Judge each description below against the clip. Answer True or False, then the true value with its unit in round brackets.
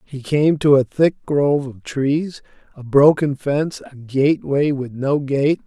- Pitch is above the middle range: False (140 Hz)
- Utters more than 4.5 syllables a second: False (4.2 syllables/s)